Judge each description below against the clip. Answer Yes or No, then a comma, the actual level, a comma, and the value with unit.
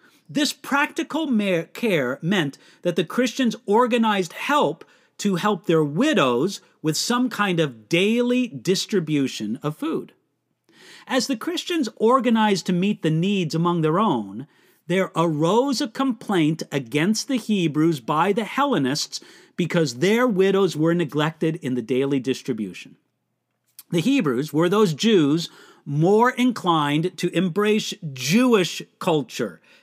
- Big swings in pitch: Yes, wide, 6.7 semitones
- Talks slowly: Yes, slow, 125 wpm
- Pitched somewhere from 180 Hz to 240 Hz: Yes, high, 190 Hz